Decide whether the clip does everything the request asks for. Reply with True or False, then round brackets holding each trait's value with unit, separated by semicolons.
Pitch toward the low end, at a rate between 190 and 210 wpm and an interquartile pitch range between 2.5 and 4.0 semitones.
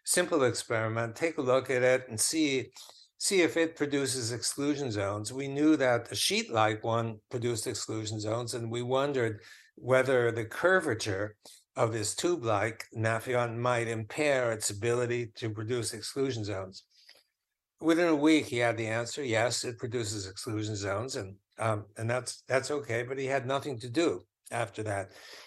False (120 Hz; 165 wpm; 3.5 semitones)